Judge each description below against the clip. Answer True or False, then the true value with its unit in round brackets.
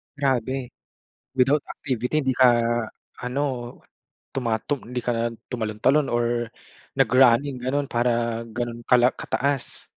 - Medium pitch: False (125 Hz)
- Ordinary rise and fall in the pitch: False (2.3 semitones)